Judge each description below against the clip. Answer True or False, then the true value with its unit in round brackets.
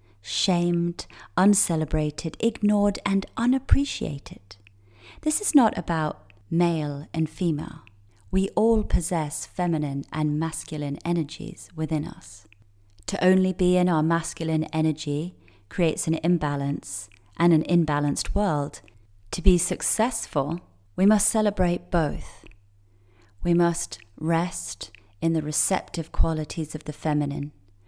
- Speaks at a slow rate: True (110 wpm)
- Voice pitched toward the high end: False (160 Hz)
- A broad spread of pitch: True (7.7 semitones)